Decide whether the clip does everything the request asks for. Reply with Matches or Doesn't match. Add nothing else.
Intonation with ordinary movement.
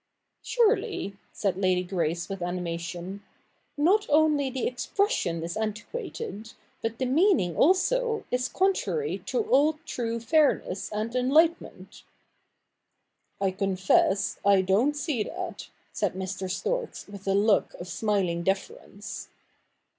Doesn't match